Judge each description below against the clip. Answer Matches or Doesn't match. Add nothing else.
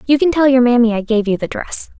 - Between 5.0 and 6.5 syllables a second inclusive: Matches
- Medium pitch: Doesn't match